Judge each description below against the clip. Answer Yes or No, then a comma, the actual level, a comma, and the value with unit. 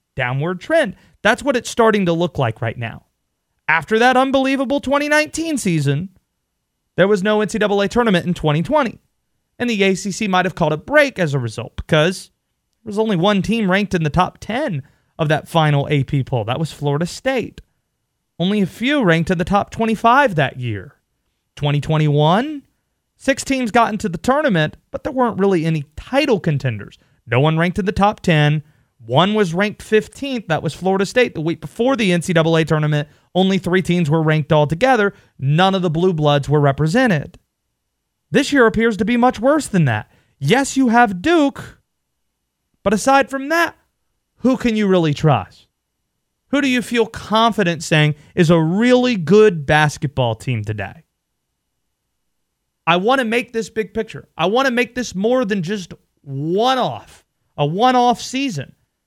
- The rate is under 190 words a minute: Yes, average, 170 wpm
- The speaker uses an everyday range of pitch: No, wide, 7.6 semitones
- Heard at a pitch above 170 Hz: Yes, medium, 185 Hz